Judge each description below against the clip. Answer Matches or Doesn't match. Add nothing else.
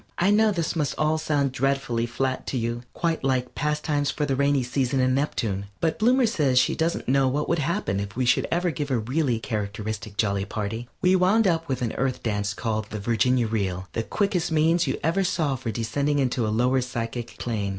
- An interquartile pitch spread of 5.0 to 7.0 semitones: Matches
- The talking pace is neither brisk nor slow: Doesn't match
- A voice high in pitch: Doesn't match